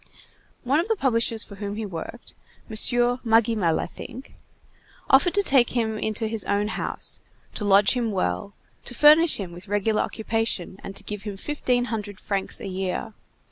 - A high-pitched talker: Yes, high, 220 Hz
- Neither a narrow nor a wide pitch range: Yes, average, 3.2 semitones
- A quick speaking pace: No, average, 175 wpm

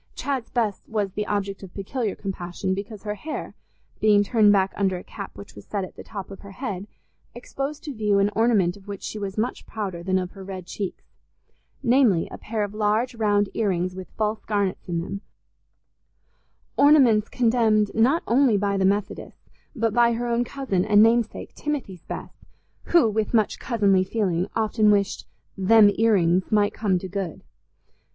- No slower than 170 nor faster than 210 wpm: Yes, average, 180 wpm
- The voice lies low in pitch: No, high, 205 Hz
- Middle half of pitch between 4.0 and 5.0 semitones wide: No, average, 2.8 semitones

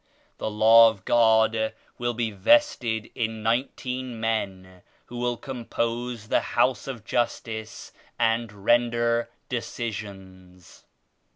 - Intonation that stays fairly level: Yes, narrow, 1.7 semitones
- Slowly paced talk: Yes, slow, 105 wpm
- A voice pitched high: No, low, 115 Hz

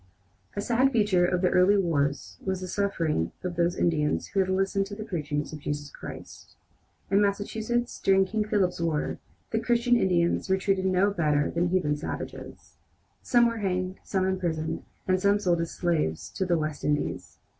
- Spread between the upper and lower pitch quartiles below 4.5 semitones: Yes, average, 3.2 semitones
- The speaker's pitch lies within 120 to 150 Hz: No, medium, 185 Hz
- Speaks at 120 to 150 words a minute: No, average, 180 wpm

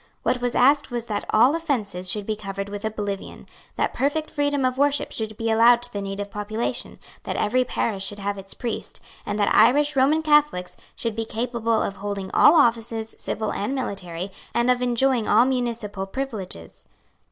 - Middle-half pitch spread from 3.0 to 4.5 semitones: Yes, average, 3.9 semitones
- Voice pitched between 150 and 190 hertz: No, high, 225 Hz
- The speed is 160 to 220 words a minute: Yes, average, 180 wpm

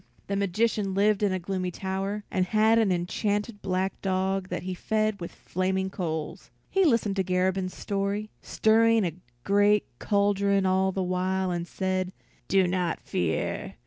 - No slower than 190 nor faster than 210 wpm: No, average, 155 wpm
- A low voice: No, high, 190 Hz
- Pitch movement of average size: No, narrow, 1.8 semitones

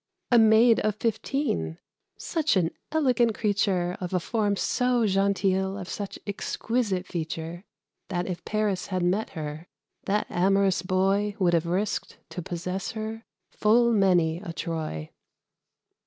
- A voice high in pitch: Yes, high, 195 Hz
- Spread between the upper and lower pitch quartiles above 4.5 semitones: No, average, 3.5 semitones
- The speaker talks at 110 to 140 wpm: Yes, slow, 135 wpm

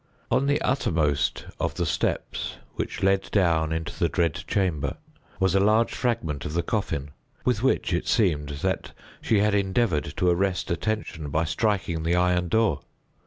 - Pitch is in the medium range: No, very low, 90 Hz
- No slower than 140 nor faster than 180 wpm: Yes, average, 165 wpm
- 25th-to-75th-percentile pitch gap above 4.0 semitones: Yes, average, 4.8 semitones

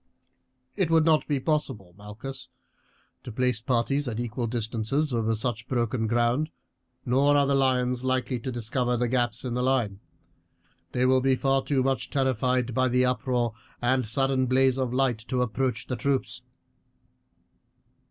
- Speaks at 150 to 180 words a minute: Yes, average, 160 wpm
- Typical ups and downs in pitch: No, narrow, 2.1 semitones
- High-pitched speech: No, low, 125 Hz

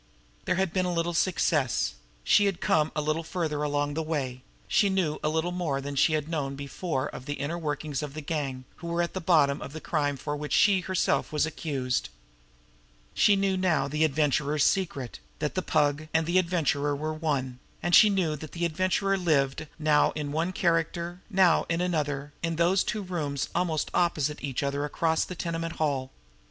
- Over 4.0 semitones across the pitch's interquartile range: No, average, 3.1 semitones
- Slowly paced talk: No, average, 195 wpm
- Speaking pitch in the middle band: Yes, medium, 155 Hz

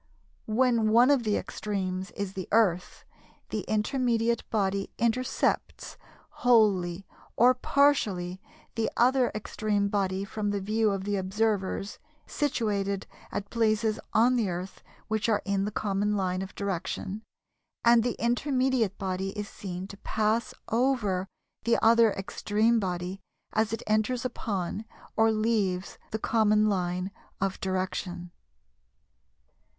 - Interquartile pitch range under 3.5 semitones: Yes, average, 2.9 semitones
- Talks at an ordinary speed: No, slow, 125 wpm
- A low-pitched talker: No, high, 210 Hz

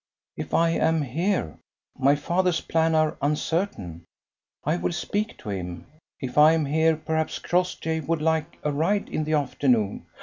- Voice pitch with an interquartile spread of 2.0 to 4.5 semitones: Yes, average, 2.7 semitones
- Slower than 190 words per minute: Yes, average, 160 wpm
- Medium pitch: Yes, medium, 155 Hz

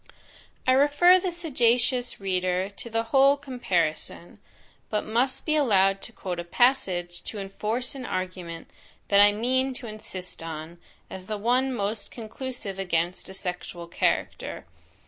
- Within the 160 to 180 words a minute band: No, average, 145 wpm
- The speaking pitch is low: No, high, 215 Hz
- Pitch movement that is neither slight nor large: No, wide, 5.7 semitones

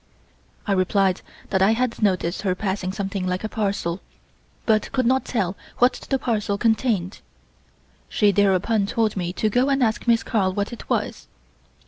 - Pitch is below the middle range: No, high, 205 Hz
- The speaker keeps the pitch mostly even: No, average, 3.2 semitones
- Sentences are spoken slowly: No, average, 165 wpm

